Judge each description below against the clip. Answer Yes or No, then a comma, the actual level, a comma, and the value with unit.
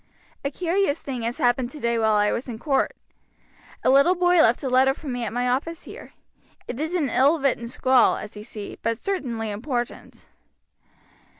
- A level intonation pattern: No, average, 3.9 semitones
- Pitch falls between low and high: No, very high, 255 Hz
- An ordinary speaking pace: Yes, average, 185 wpm